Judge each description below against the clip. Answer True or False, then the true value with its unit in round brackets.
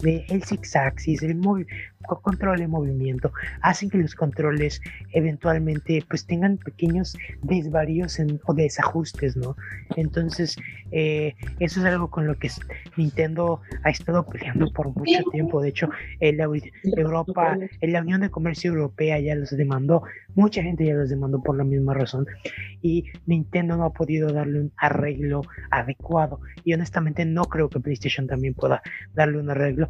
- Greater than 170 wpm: False (160 wpm)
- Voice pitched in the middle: True (155 Hz)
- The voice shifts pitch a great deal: False (2.8 semitones)